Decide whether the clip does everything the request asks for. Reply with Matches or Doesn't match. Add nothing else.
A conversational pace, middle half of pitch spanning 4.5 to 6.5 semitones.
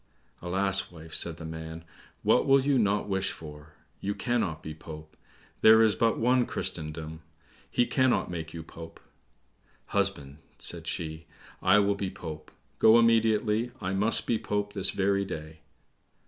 Matches